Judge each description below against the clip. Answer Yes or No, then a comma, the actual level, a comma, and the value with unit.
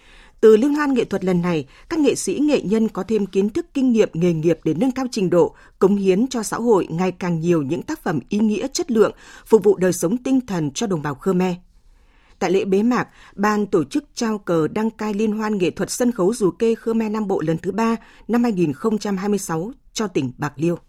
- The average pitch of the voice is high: Yes, high, 210 Hz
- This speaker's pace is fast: No, average, 235 wpm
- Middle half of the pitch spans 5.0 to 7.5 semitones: No, average, 4.1 semitones